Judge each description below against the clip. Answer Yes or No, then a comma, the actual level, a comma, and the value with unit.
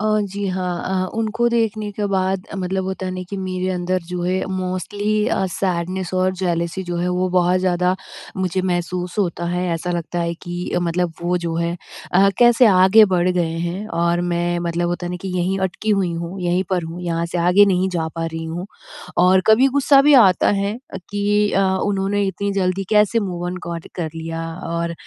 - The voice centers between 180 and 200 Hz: Yes, medium, 185 Hz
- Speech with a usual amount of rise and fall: No, narrow, 1.8 semitones